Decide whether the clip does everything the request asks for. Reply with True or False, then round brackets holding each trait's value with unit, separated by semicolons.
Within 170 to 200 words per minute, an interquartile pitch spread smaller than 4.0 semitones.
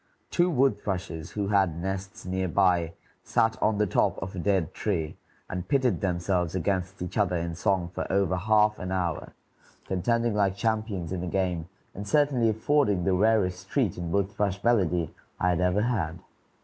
True (175 wpm; 3.1 semitones)